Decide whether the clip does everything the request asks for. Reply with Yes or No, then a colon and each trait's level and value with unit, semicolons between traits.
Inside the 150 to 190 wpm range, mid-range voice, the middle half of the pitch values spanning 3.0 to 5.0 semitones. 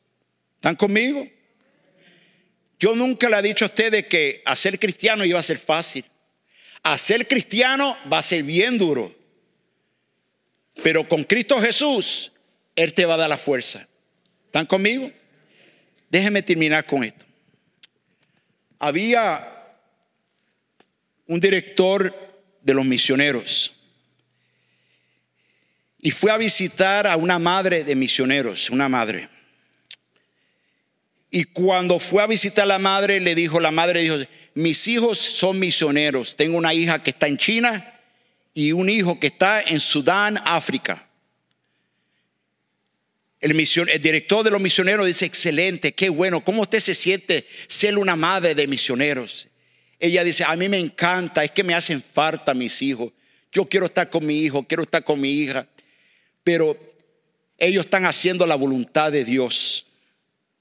No: average, 140 wpm; medium, 175 Hz; average, 4.5 semitones